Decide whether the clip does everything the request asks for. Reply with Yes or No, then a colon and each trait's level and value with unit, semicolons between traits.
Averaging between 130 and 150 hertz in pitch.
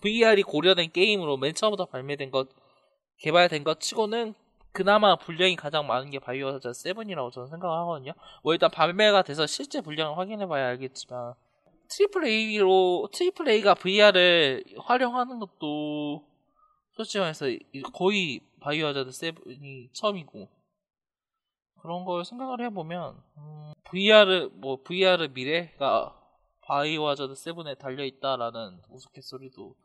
No: medium, 170 Hz